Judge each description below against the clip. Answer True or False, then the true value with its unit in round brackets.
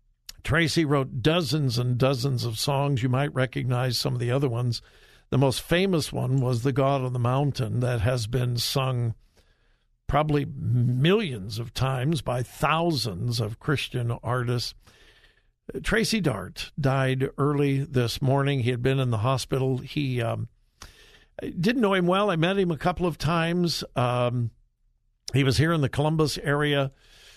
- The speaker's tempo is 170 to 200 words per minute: False (155 wpm)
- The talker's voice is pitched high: False (135 Hz)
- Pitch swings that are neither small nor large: True (3.3 semitones)